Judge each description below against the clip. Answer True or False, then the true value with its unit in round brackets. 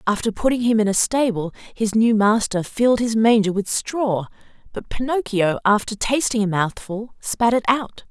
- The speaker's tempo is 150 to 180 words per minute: True (170 wpm)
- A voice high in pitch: True (220 Hz)